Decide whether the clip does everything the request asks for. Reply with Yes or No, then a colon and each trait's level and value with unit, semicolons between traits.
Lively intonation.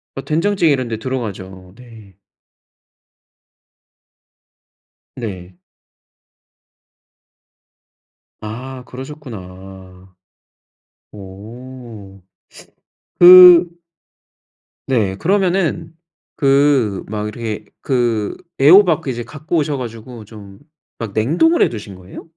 Yes: wide, 6.3 semitones